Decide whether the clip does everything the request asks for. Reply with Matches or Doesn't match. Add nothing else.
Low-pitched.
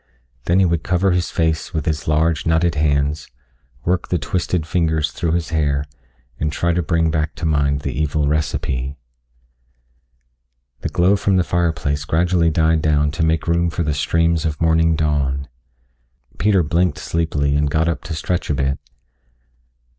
Matches